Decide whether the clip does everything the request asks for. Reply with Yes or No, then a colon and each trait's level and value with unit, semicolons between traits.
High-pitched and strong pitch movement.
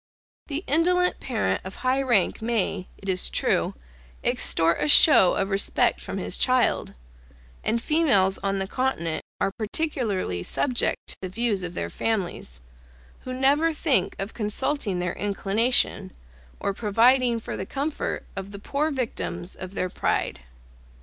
Yes: high, 215 Hz; wide, 5.7 semitones